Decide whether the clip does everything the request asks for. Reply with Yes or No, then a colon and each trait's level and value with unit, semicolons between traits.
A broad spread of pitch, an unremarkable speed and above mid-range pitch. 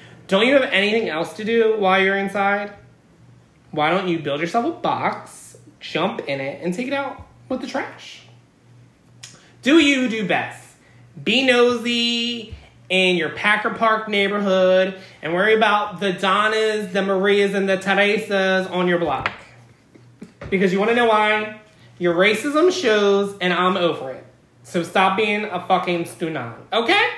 No: average, 3.5 semitones; average, 155 wpm; high, 200 Hz